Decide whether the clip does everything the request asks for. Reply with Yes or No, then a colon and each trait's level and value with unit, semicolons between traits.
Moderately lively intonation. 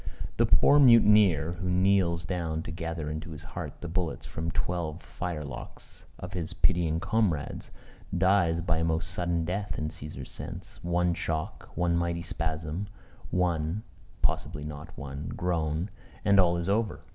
No: narrow, 2.3 semitones